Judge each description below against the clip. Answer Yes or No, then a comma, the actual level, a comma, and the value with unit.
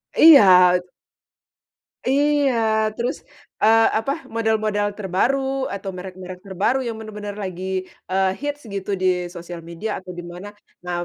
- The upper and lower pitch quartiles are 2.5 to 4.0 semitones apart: Yes, average, 3.7 semitones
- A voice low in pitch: No, high, 205 Hz